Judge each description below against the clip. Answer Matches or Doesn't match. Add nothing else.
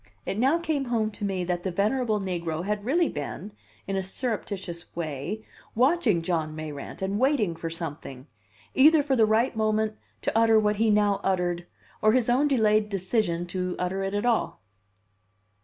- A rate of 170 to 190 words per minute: Matches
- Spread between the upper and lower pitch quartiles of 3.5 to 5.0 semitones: Matches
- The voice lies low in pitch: Doesn't match